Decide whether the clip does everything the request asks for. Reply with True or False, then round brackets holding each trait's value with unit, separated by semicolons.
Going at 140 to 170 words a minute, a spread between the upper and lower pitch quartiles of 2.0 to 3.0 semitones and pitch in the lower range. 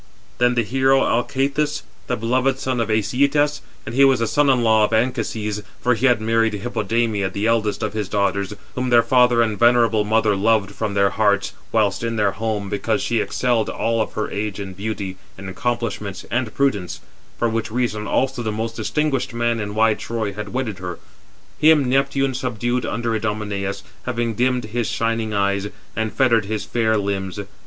False (180 wpm; 2.7 semitones; 115 Hz)